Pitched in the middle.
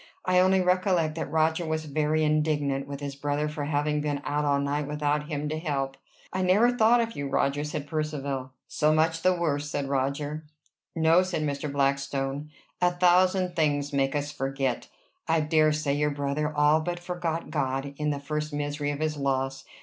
Yes: medium, 150 Hz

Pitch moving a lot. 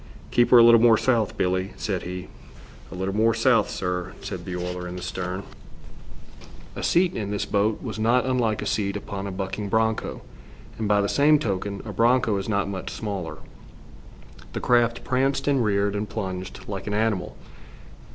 No: average, 3.4 semitones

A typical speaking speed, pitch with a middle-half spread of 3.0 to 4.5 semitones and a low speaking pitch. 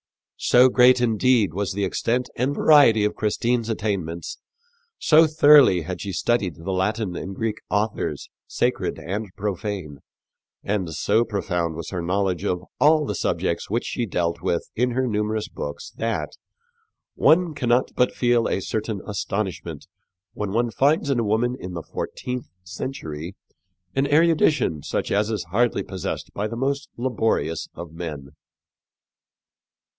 No: average, 145 wpm; average, 5.0 semitones; low, 105 Hz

